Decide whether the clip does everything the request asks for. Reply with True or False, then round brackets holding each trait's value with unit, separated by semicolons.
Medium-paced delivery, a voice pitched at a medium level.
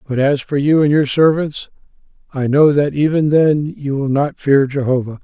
True (195 wpm; 145 Hz)